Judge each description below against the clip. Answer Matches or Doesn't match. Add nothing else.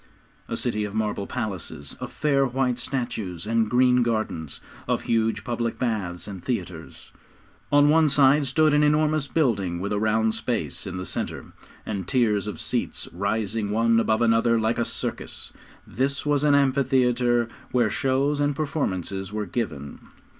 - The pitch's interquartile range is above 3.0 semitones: Matches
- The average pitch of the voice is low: Matches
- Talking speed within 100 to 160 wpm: Matches